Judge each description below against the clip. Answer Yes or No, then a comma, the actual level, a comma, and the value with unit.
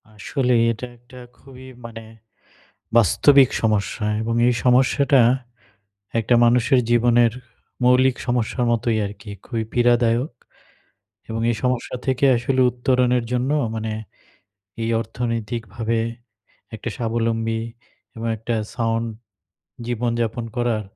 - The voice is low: Yes, low, 120 Hz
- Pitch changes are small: Yes, narrow, 1.7 semitones